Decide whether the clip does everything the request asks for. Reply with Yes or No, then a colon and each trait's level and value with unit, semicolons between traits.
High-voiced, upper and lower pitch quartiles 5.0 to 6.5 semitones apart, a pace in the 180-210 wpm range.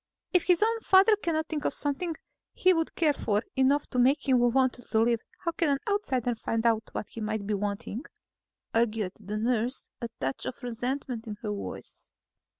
Yes: high, 245 Hz; wide, 5.6 semitones; average, 190 wpm